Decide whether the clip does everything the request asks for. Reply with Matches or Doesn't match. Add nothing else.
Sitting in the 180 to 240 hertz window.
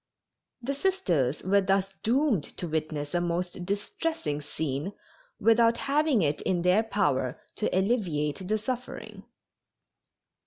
Matches